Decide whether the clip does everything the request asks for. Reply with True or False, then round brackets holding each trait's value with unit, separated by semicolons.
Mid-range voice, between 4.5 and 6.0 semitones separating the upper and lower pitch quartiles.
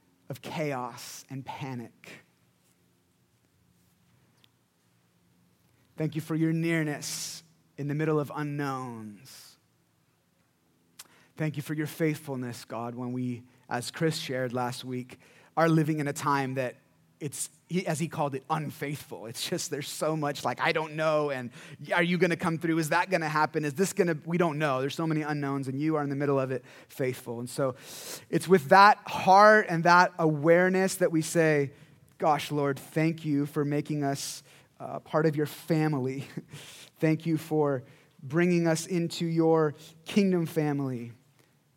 False (150 Hz; 3.0 semitones)